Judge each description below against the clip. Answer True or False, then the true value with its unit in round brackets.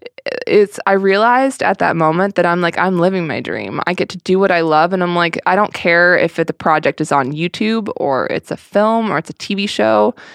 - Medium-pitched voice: True (180 Hz)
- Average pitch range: True (3.7 semitones)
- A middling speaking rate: False (240 wpm)